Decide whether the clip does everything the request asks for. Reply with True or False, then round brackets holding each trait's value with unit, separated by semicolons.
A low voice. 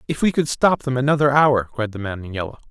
True (130 Hz)